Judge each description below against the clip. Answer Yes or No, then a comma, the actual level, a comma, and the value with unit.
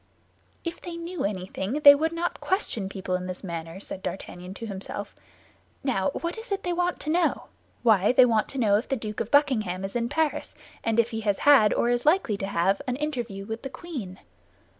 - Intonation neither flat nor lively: No, wide, 7.4 semitones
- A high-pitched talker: Yes, high, 230 Hz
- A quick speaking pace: Yes, fast, 210 wpm